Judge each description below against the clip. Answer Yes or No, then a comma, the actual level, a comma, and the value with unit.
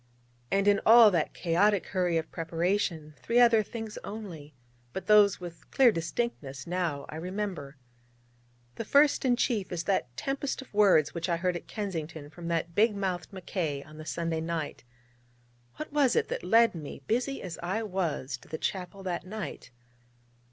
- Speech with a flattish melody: No, average, 4.5 semitones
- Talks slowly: No, average, 170 wpm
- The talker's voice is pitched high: No, medium, 180 Hz